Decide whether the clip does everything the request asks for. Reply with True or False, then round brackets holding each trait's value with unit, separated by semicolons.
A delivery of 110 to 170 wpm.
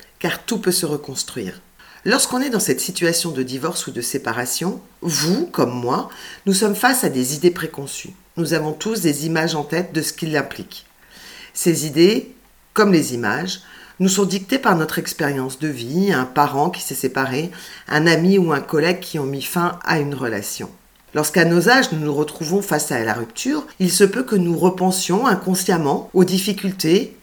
False (185 wpm)